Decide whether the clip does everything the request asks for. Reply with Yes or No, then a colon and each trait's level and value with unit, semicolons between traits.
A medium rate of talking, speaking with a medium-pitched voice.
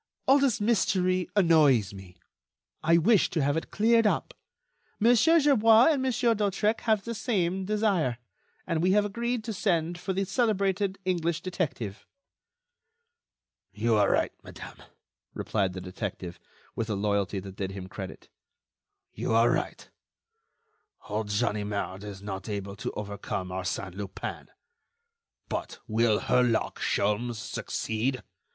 No: slow, 130 wpm; medium, 155 Hz